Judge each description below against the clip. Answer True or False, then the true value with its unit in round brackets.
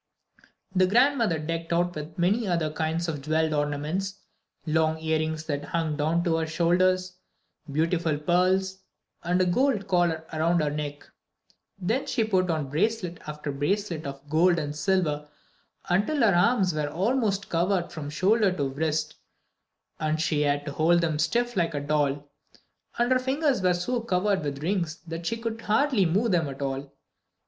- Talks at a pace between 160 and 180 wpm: True (165 wpm)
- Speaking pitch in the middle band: True (170 Hz)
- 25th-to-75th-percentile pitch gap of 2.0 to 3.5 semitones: False (3.9 semitones)